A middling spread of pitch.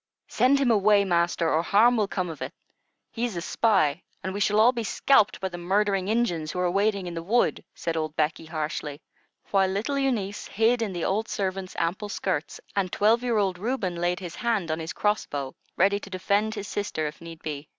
Yes: average, 4.0 semitones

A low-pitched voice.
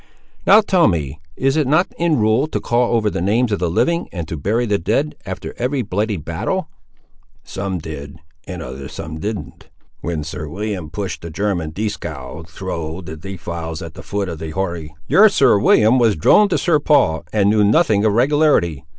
Yes: low, 100 Hz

